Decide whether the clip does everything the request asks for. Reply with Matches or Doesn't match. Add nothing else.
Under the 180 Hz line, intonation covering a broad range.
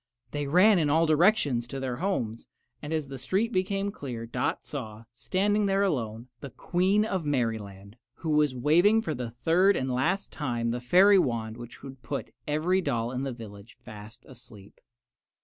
Matches